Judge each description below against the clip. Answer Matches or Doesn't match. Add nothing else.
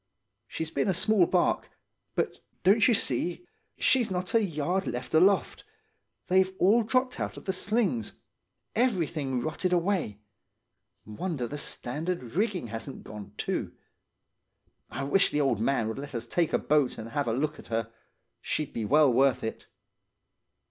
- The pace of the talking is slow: Doesn't match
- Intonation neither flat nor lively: Doesn't match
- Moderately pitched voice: Matches